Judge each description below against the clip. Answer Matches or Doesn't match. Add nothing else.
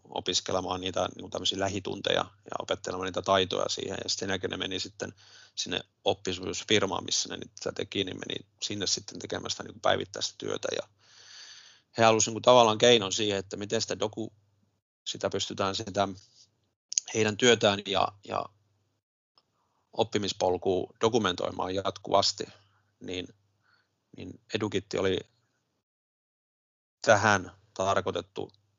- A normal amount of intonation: Doesn't match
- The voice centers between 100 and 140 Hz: Matches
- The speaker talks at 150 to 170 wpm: Doesn't match